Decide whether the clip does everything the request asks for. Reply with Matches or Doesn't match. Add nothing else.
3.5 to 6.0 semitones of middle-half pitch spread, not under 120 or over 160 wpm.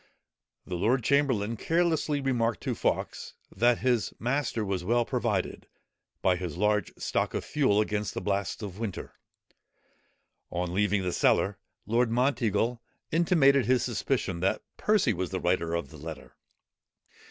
Matches